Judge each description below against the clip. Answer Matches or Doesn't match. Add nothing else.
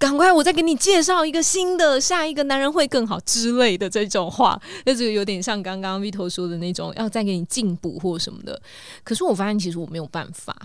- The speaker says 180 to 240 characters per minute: Doesn't match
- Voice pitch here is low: Doesn't match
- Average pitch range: Doesn't match